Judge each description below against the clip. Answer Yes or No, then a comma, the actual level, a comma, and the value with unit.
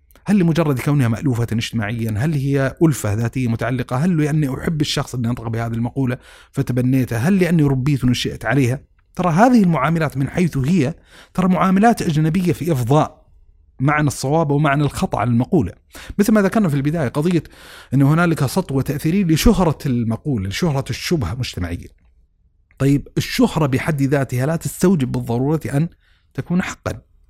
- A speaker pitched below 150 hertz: Yes, medium, 140 Hz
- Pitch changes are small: No, average, 5.3 semitones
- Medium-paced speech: No, fast, 150 wpm